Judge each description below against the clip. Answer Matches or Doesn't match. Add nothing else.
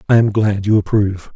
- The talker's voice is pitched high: Doesn't match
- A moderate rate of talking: Doesn't match